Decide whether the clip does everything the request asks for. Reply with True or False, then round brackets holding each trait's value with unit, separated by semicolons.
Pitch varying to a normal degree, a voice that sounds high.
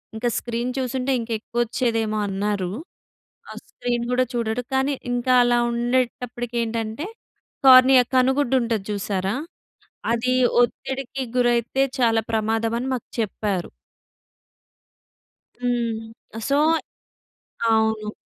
False (2.3 semitones; 235 Hz)